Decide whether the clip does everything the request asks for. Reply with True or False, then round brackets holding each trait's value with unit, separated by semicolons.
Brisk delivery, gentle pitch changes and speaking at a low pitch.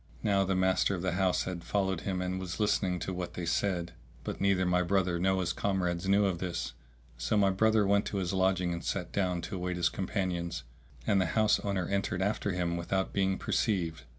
True (210 wpm; 1.9 semitones; 95 Hz)